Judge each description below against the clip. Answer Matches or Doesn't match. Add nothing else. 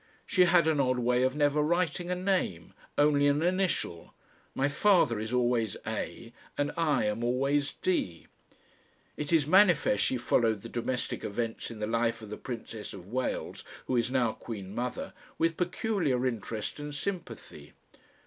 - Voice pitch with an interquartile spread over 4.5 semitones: Matches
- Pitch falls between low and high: Doesn't match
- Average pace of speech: Matches